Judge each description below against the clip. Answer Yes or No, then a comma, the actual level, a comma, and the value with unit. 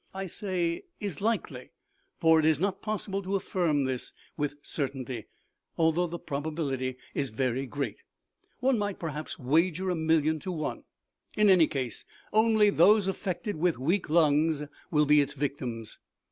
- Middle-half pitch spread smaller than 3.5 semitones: No, average, 5.0 semitones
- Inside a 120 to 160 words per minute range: Yes, average, 145 wpm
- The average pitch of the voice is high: No, medium, 160 Hz